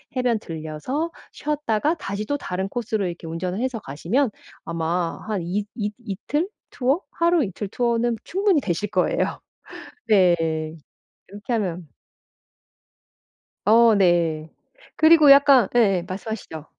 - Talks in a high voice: Yes, high, 210 Hz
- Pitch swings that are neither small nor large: No, wide, 6.3 semitones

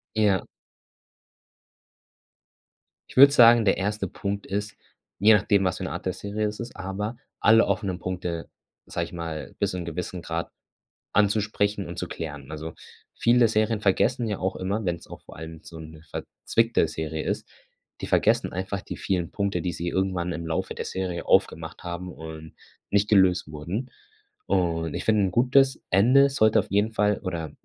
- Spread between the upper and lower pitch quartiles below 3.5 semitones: No, average, 3.8 semitones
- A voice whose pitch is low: Yes, very low, 95 Hz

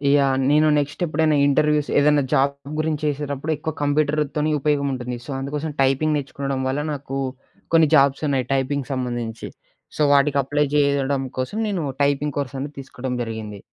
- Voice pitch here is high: No, medium, 140 Hz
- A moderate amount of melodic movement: No, narrow, 1.9 semitones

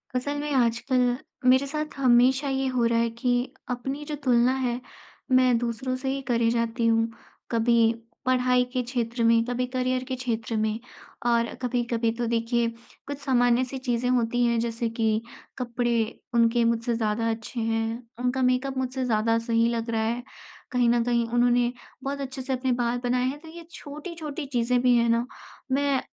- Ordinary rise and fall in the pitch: No, narrow, 1.8 semitones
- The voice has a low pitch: No, high, 245 Hz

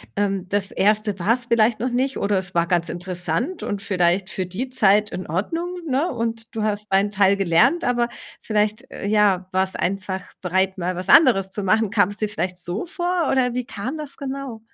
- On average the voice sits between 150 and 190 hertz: No, high, 205 Hz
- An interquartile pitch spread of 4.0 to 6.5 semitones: Yes, average, 4.3 semitones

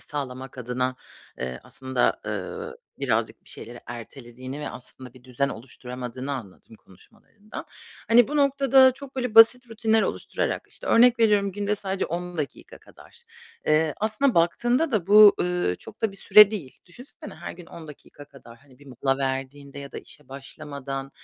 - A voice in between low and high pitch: Yes, medium, 150 Hz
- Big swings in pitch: Yes, wide, 8.8 semitones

